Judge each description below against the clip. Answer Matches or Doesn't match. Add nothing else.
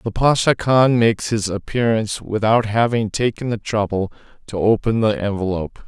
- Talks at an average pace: Matches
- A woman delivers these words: Doesn't match